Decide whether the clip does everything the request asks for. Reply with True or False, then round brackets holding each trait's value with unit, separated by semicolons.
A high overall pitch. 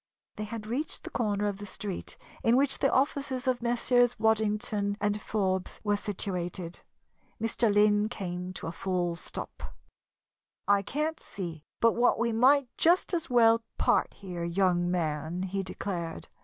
True (205 Hz)